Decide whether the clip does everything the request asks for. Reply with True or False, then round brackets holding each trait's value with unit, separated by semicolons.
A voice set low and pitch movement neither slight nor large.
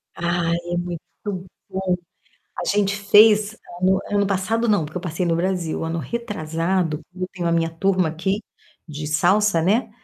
False (185 Hz; 3.4 semitones)